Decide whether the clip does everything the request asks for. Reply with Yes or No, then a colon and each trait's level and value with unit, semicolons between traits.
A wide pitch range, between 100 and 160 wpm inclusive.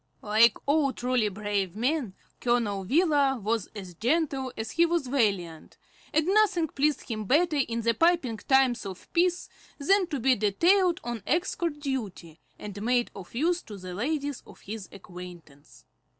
Yes: wide, 7.0 semitones; average, 155 wpm